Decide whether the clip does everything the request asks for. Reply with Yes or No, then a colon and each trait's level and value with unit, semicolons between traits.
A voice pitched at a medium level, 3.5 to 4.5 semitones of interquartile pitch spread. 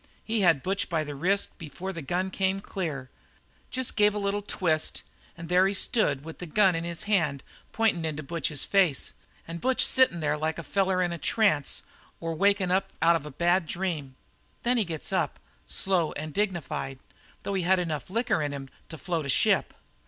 Yes: medium, 175 Hz; average, 3.9 semitones